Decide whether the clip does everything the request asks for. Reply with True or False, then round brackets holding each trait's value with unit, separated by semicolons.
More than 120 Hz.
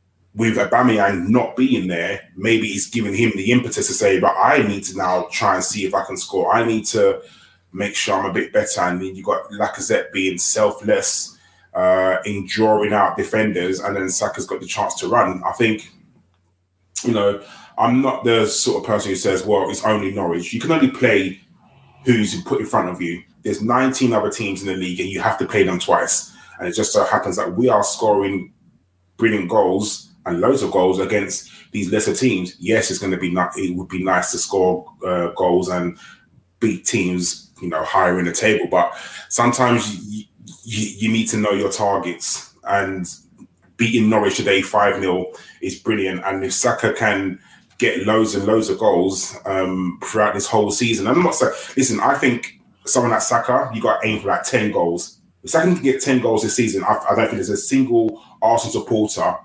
False (100 Hz)